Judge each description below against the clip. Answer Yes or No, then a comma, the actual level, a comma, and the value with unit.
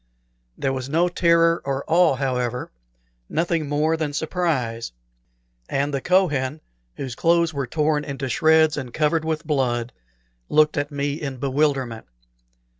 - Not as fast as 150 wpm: Yes, slow, 135 wpm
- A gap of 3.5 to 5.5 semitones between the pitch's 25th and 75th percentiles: No, average, 3.1 semitones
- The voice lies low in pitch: No, medium, 145 Hz